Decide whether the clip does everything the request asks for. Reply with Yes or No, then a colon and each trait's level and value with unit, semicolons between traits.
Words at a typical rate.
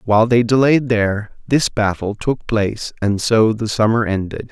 Yes: average, 175 wpm